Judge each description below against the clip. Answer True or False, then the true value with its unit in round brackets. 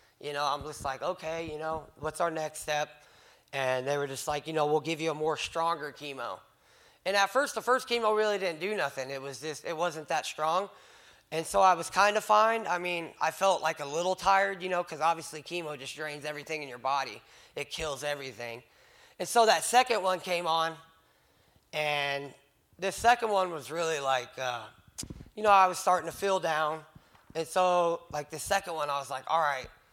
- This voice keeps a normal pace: False (215 wpm)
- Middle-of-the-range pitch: True (160 Hz)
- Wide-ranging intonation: False (3.9 semitones)